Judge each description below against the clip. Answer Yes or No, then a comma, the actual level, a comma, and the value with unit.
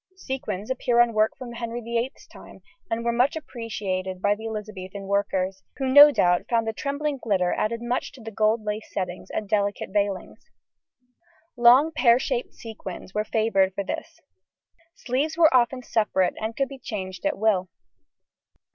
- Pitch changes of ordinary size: Yes, average, 3.6 semitones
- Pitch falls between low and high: No, high, 225 Hz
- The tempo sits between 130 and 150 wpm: No, average, 165 wpm